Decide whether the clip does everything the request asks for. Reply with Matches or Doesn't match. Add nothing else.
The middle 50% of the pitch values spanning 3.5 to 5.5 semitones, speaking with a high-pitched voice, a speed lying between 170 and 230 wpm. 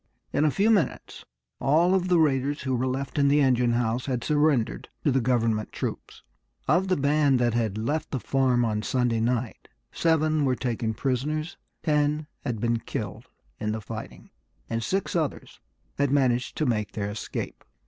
Doesn't match